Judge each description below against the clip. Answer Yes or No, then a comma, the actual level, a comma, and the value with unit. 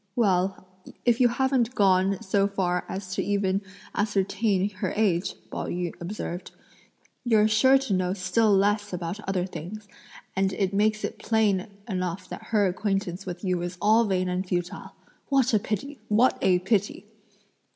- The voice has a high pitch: Yes, high, 195 Hz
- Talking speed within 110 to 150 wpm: No, average, 160 wpm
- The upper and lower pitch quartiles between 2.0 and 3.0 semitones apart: Yes, average, 2.7 semitones